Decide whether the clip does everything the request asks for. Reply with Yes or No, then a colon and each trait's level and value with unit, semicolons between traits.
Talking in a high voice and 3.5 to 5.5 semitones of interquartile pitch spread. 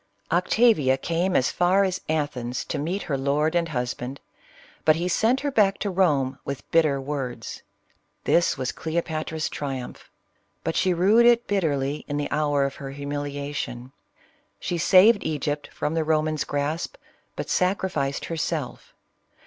No: medium, 155 Hz; average, 4.2 semitones